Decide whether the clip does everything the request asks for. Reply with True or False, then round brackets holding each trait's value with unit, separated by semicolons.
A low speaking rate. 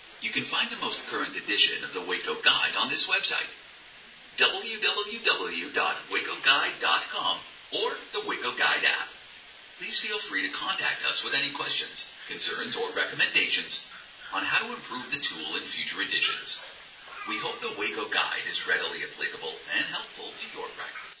False (155 wpm)